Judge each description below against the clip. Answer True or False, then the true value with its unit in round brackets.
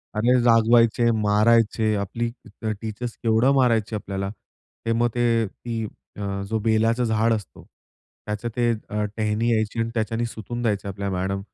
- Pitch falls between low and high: False (110 Hz)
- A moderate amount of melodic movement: False (1.9 semitones)